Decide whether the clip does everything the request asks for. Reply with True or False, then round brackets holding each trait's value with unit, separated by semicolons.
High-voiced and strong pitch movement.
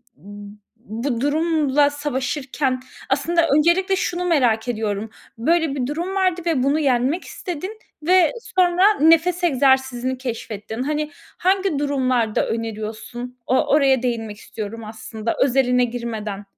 True (265 Hz; 5.8 semitones)